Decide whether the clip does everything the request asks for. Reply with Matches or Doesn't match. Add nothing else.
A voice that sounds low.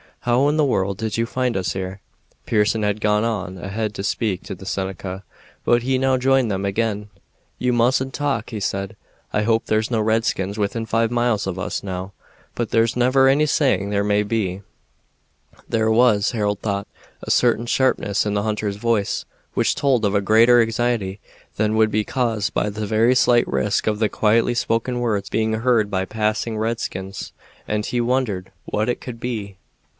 Matches